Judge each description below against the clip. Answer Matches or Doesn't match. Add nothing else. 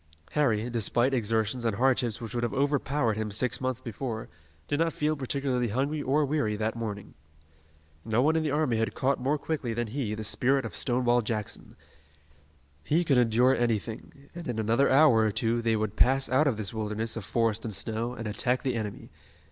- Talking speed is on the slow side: Doesn't match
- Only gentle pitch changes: Doesn't match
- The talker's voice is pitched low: Matches